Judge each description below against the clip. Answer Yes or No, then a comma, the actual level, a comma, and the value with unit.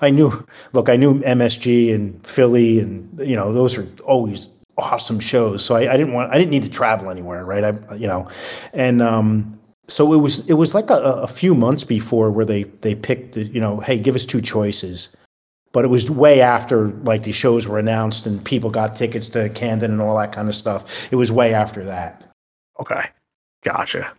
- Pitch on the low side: Yes, low, 115 Hz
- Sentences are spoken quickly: Yes, fast, 210 wpm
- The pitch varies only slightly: No, average, 3.1 semitones